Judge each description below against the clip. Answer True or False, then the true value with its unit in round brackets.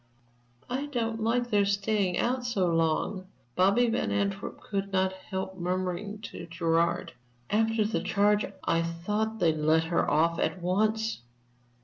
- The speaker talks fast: False (140 wpm)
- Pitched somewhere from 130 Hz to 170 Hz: False (195 Hz)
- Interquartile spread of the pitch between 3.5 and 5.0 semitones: True (4.0 semitones)